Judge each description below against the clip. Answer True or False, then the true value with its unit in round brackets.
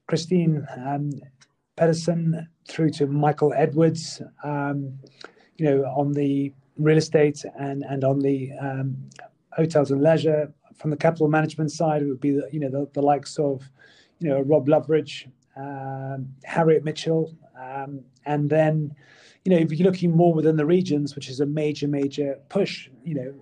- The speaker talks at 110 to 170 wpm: True (165 wpm)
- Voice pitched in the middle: True (145 Hz)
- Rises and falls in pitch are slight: True (2.2 semitones)